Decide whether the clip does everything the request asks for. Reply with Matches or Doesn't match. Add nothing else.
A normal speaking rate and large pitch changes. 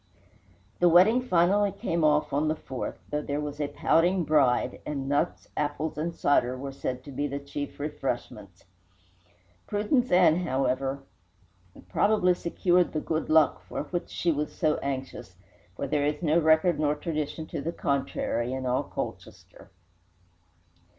Doesn't match